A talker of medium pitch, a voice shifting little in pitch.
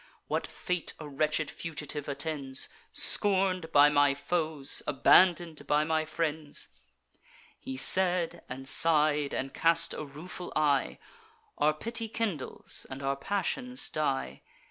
No: medium, 155 Hz; average, 3.5 semitones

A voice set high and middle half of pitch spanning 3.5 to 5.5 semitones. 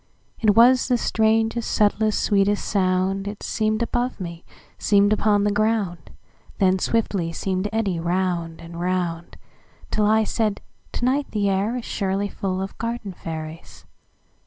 No: high, 200 Hz; average, 3.1 semitones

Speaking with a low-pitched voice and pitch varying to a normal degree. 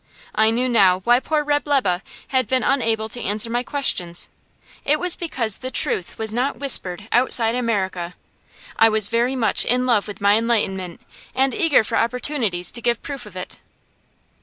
No: high, 230 Hz; average, 4.1 semitones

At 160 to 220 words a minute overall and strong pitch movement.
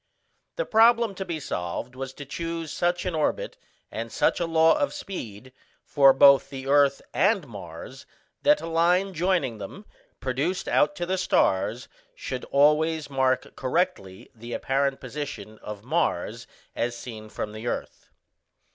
No: average, 150 wpm; wide, 5.9 semitones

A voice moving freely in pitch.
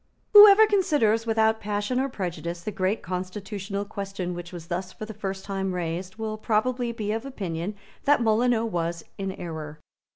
No: average, 3.8 semitones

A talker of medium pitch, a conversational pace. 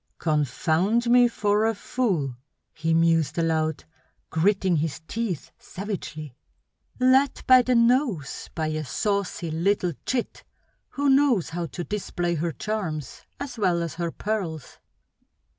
No: medium, 180 Hz; slow, 125 wpm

